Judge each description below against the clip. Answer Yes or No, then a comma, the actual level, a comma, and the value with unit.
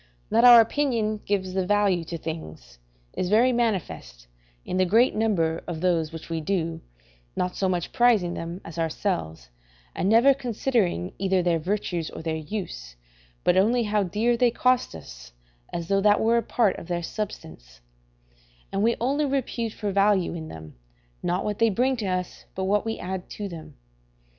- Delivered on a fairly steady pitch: No, average, 5.1 semitones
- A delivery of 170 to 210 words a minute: Yes, average, 175 wpm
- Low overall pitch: No, high, 190 Hz